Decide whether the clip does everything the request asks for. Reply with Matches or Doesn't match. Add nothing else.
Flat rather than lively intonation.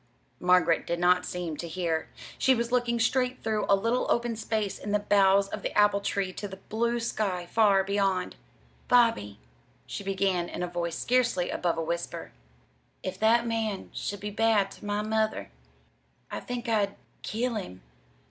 Doesn't match